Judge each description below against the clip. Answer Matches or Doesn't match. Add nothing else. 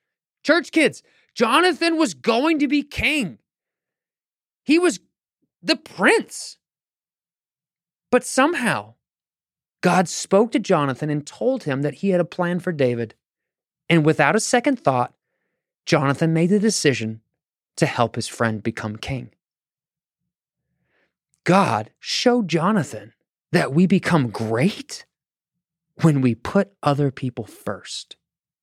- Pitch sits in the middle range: Matches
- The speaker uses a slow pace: Matches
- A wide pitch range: Matches